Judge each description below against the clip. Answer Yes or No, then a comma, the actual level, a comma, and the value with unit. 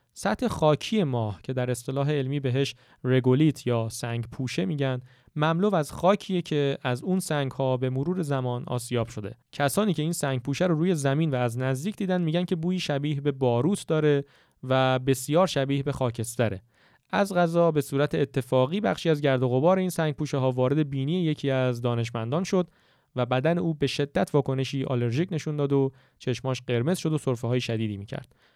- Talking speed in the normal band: No, fast, 185 wpm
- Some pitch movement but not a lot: Yes, average, 4.2 semitones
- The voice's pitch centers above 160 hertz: No, medium, 140 Hz